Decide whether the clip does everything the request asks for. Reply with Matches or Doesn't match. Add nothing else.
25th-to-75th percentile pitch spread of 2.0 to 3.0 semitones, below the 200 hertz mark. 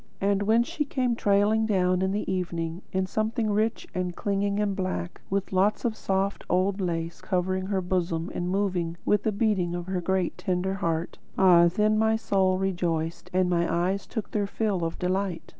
Matches